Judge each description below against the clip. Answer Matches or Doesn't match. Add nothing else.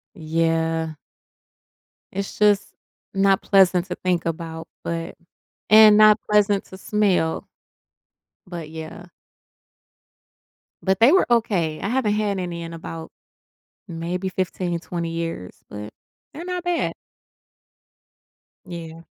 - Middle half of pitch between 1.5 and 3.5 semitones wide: Doesn't match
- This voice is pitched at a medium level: Matches